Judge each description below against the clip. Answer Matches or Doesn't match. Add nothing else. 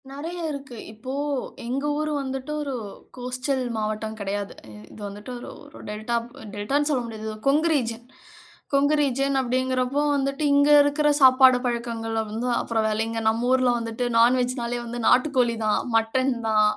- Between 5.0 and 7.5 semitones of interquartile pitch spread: Doesn't match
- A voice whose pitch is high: Matches